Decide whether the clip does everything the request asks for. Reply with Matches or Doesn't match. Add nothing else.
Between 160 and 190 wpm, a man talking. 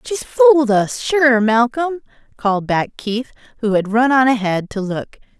Doesn't match